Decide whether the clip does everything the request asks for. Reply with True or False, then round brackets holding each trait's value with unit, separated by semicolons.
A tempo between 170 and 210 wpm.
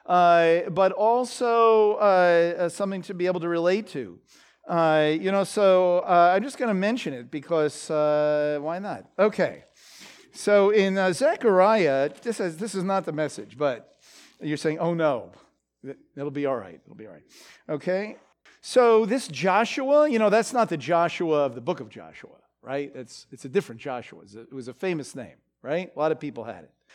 True (190 wpm)